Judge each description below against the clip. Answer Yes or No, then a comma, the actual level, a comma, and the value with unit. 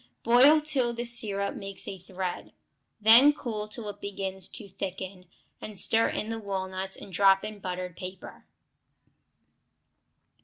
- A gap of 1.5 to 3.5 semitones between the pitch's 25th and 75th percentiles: Yes, average, 3.1 semitones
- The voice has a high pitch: Yes, high, 200 Hz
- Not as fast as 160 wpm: Yes, average, 140 wpm